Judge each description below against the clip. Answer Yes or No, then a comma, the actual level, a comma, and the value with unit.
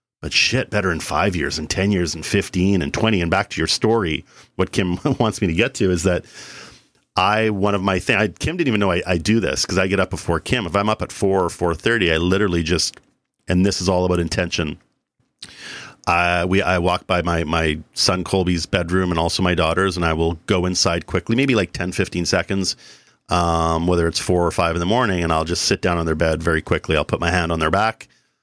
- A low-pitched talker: Yes, very low, 90 Hz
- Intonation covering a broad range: No, average, 2.8 semitones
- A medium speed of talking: No, fast, 240 wpm